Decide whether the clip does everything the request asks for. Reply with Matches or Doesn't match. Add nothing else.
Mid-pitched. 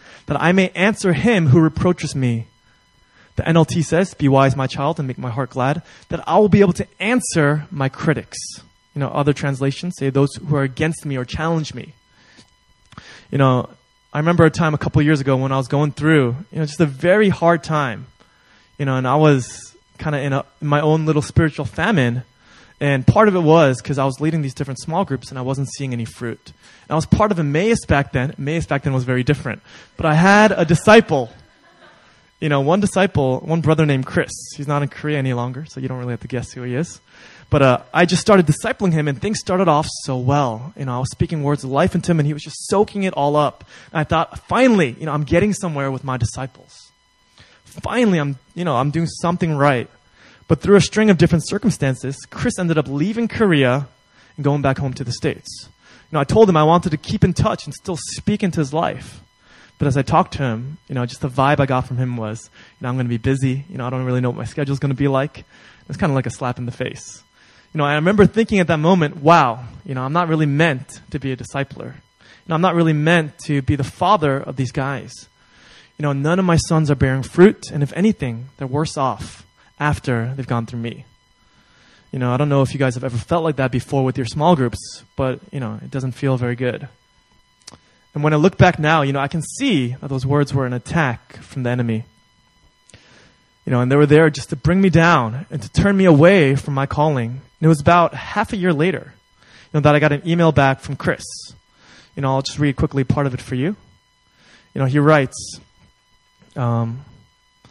Matches